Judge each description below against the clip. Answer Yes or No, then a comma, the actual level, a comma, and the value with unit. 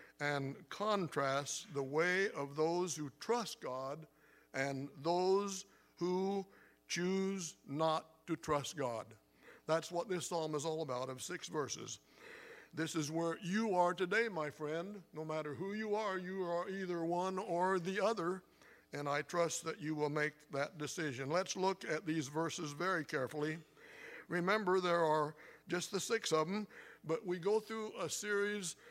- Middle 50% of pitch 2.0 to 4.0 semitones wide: Yes, average, 3.7 semitones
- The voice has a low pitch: No, medium, 170 Hz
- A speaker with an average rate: Yes, average, 160 wpm